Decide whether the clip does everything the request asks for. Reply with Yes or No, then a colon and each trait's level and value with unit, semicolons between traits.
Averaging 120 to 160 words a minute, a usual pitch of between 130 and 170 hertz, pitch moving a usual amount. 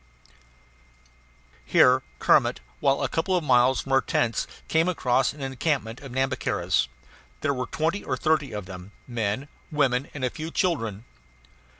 Yes: average, 150 wpm; low, 135 Hz; average, 4.2 semitones